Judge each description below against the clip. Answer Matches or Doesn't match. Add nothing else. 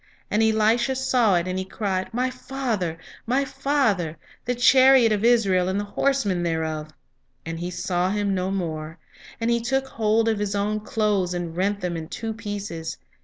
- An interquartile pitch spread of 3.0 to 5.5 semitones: Matches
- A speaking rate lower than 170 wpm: Doesn't match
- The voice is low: Doesn't match